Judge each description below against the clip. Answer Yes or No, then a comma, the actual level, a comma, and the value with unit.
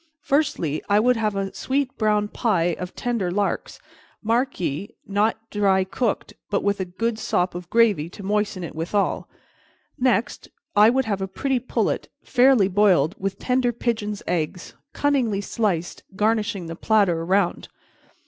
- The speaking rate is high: No, average, 150 wpm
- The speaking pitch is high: Yes, high, 205 Hz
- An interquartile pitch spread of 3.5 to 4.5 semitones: Yes, average, 3.8 semitones